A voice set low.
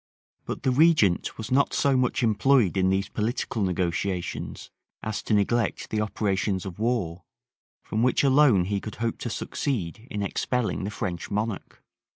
Yes: low, 105 Hz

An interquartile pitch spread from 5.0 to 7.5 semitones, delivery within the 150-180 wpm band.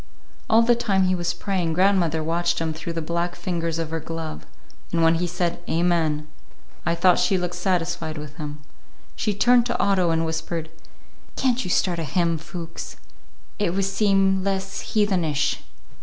No: average, 2.8 semitones; average, 170 wpm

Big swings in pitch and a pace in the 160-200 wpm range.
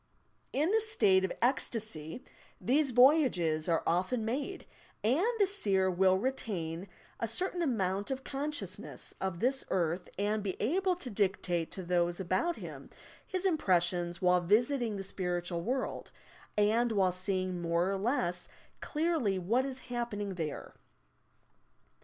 No: wide, 6.5 semitones; slow, 135 wpm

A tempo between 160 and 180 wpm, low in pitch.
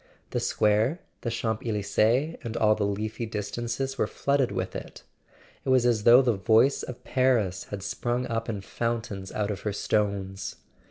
Yes: average, 170 wpm; low, 110 Hz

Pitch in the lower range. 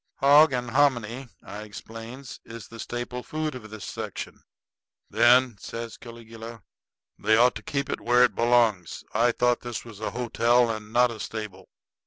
Yes: low, 120 Hz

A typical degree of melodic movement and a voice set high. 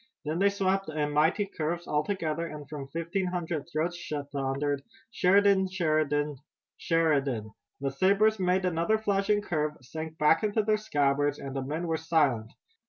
No: average, 4.4 semitones; medium, 160 Hz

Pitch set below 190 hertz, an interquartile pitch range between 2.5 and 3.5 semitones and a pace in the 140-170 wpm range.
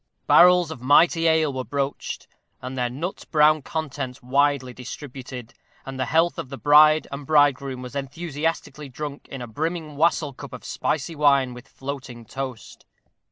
Yes: medium, 140 Hz; average, 3.0 semitones; average, 160 wpm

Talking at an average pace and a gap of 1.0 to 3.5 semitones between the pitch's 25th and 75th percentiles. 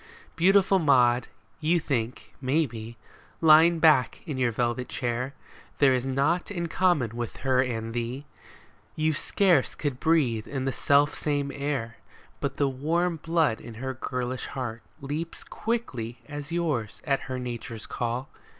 No: average, 150 wpm; average, 4.5 semitones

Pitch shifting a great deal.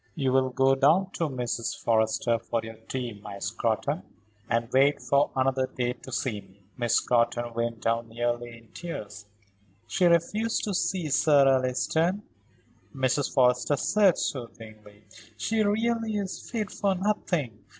Yes: wide, 6.4 semitones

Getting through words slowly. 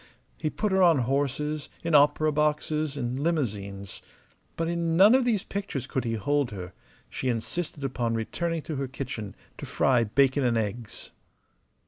No: average, 160 wpm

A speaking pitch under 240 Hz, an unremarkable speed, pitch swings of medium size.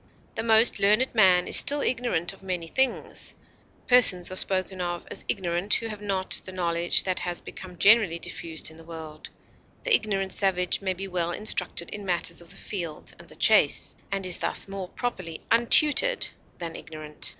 Yes: medium, 185 Hz; average, 180 wpm; average, 3.5 semitones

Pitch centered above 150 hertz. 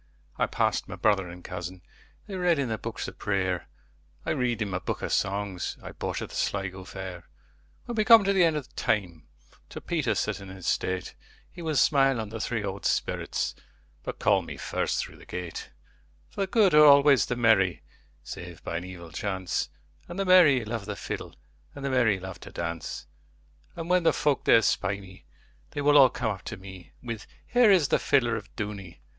No: low, 105 Hz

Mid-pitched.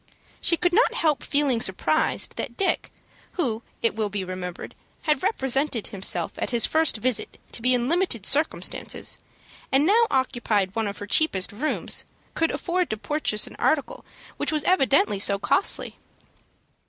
No: very high, 260 Hz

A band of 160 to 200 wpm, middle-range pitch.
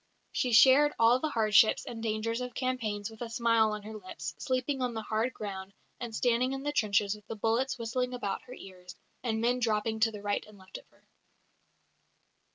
No: average, 195 wpm; high, 225 Hz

